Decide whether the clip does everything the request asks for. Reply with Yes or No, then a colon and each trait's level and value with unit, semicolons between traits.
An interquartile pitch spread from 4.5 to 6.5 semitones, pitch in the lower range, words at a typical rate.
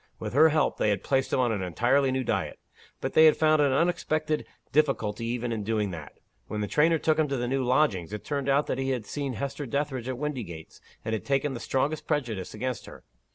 No: average, 4.8 semitones; low, 130 Hz; fast, 230 wpm